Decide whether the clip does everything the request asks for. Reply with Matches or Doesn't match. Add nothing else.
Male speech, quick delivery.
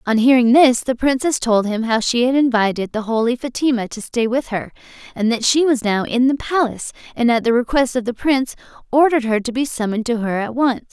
Doesn't match